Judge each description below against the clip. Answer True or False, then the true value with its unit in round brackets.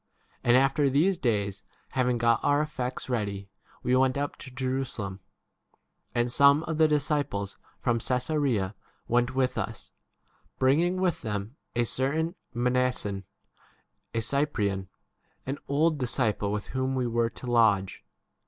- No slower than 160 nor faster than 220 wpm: False (140 wpm)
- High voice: False (125 Hz)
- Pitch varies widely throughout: False (3.9 semitones)